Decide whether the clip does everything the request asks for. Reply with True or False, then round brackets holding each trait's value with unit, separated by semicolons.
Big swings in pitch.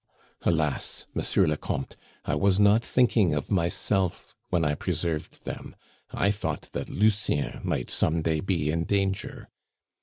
False (4.5 semitones)